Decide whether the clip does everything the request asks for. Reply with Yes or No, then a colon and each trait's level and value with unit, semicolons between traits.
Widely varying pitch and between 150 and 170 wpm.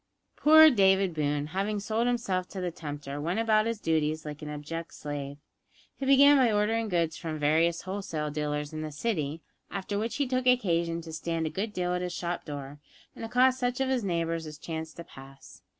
No: wide, 6.1 semitones; average, 200 wpm